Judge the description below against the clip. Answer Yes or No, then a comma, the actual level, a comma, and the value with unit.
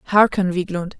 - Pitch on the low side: No, medium, 185 Hz